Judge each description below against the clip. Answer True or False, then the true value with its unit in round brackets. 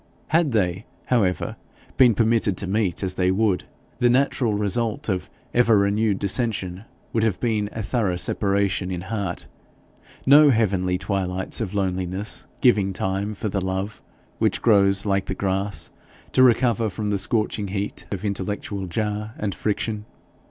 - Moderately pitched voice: False (100 Hz)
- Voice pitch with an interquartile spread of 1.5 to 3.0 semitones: True (2.7 semitones)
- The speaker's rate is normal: True (150 wpm)